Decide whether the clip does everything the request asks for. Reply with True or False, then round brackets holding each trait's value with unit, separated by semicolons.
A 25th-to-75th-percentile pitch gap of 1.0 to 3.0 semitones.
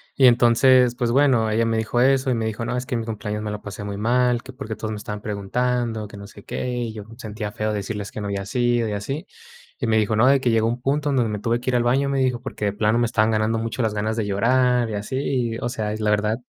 True (2.7 semitones)